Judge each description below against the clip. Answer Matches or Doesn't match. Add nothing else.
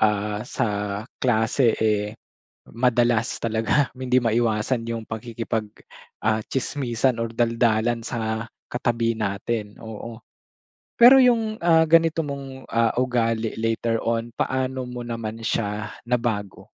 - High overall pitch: Doesn't match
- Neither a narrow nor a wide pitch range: Doesn't match